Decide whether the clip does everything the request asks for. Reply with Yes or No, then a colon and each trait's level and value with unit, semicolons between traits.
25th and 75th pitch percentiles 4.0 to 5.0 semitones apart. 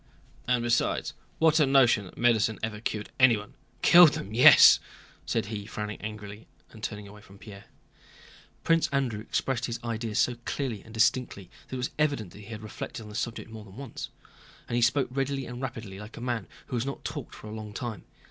No: average, 3.1 semitones